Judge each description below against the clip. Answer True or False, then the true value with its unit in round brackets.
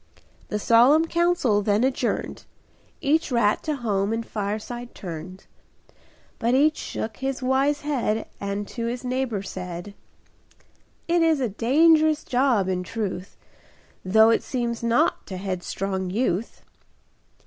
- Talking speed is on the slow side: True (125 wpm)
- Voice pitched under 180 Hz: False (230 Hz)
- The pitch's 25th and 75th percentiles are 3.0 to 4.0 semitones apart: False (5.1 semitones)